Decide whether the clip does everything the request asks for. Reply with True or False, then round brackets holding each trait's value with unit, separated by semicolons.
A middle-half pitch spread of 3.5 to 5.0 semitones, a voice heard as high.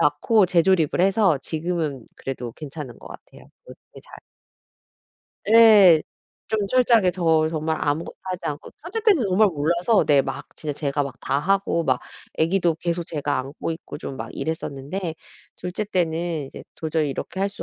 False (4.5 semitones; 165 Hz)